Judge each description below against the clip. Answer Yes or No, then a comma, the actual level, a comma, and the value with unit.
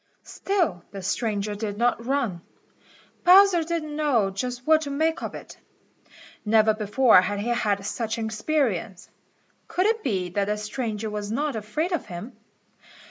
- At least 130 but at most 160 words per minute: Yes, average, 155 wpm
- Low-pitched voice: No, high, 225 Hz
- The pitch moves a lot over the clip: Yes, wide, 6.2 semitones